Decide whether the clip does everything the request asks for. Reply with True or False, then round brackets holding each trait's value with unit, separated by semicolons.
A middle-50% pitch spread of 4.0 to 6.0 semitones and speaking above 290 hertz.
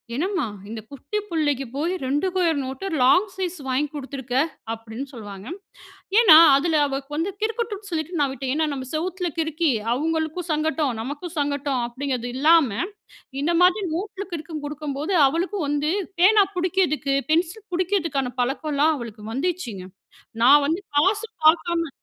True (4.5 semitones; 310 Hz)